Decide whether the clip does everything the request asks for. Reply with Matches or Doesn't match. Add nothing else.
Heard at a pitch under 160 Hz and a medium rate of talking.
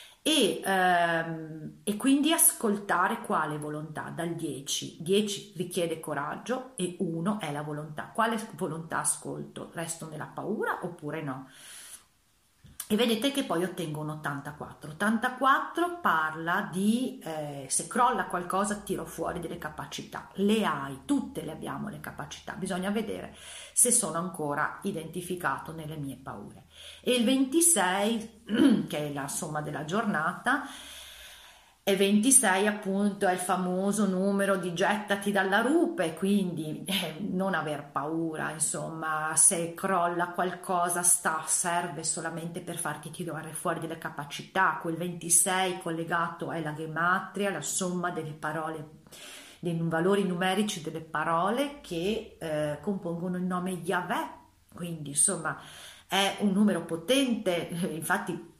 Doesn't match